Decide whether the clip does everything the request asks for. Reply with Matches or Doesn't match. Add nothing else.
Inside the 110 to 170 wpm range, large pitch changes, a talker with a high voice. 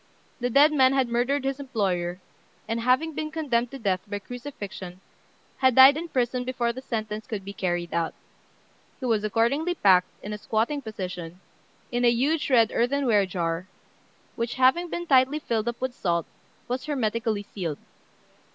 Doesn't match